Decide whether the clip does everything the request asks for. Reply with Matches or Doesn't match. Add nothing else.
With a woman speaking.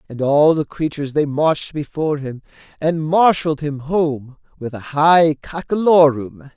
Doesn't match